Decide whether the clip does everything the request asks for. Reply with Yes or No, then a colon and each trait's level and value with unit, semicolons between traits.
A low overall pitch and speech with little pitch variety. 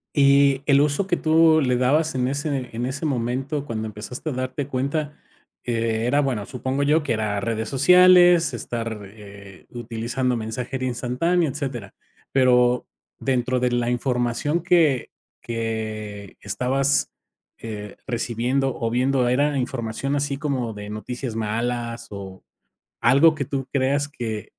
No: low, 125 Hz; average, 3.6 semitones